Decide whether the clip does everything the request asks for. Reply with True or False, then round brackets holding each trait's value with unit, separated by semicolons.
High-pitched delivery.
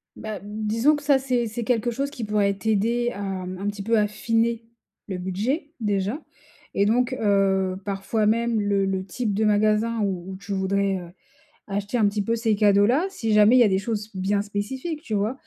True (210 Hz)